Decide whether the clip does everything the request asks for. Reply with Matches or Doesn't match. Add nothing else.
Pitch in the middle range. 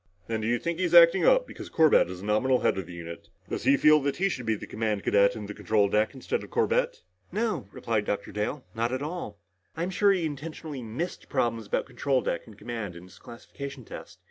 Doesn't match